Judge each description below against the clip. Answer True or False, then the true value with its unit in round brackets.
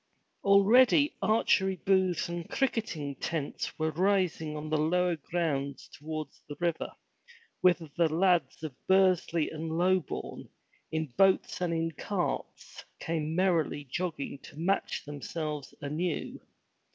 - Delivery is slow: True (120 wpm)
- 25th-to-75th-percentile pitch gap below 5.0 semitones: True (3.3 semitones)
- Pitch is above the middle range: False (165 Hz)